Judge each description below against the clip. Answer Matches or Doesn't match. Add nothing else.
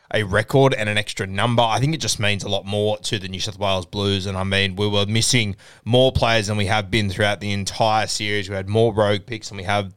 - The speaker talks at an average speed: Doesn't match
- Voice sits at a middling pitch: Doesn't match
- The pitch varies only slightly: Matches